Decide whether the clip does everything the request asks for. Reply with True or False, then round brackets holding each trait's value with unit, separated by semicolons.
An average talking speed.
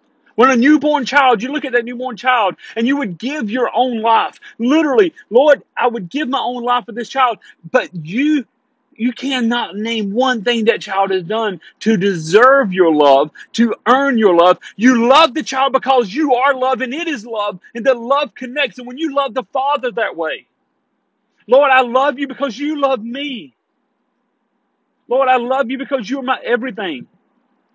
True (190 wpm)